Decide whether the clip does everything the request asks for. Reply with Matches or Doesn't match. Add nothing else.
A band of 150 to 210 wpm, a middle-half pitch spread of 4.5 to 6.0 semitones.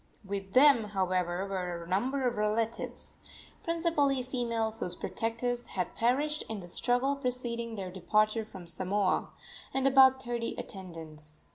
Doesn't match